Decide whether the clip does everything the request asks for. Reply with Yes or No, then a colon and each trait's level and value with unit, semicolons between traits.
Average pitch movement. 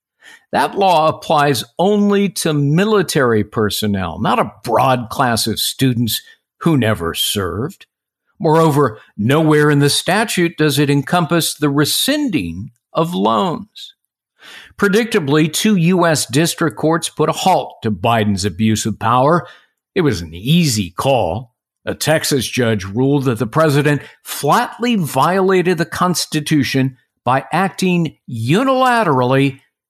No: wide, 6.1 semitones